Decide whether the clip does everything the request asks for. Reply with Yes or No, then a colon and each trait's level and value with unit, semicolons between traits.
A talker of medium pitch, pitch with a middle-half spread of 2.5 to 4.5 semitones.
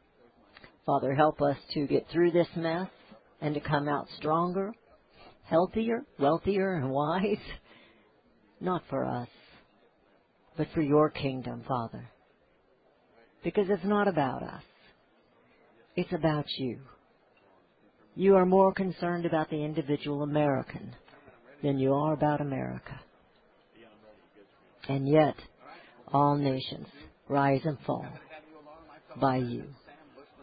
Yes: medium, 150 Hz; average, 3.9 semitones